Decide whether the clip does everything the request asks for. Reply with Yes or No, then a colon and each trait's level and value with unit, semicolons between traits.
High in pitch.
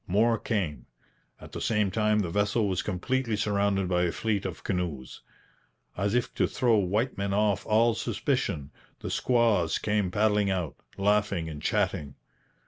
No: low, 100 Hz